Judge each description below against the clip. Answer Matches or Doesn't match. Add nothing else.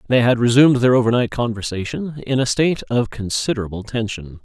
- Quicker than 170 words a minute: Doesn't match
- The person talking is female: Doesn't match